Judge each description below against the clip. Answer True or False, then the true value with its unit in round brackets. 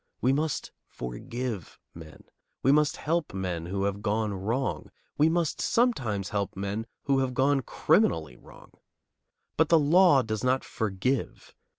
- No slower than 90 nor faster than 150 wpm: True (145 wpm)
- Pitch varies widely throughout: True (6.4 semitones)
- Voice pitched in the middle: False (120 Hz)